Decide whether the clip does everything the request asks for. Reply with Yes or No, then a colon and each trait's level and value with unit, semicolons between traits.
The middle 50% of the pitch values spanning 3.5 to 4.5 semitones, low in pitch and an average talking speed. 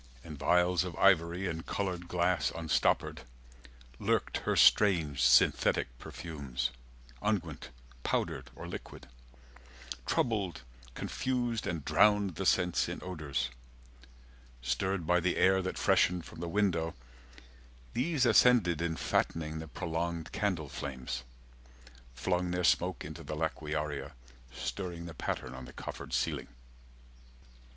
No: average, 3.8 semitones; very low, 85 Hz; slow, 120 wpm